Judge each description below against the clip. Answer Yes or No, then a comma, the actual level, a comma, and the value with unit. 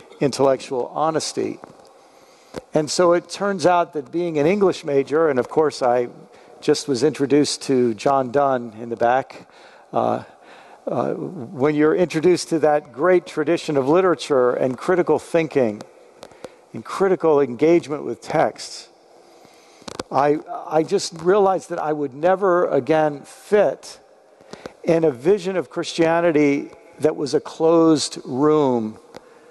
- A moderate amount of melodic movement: Yes, average, 3.7 semitones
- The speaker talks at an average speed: No, slow, 130 wpm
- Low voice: No, medium, 155 Hz